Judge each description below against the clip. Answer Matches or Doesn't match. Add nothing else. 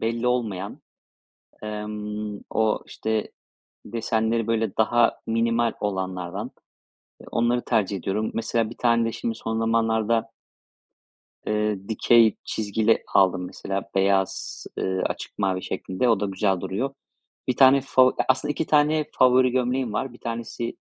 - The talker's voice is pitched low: Matches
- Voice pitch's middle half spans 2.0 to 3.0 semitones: Matches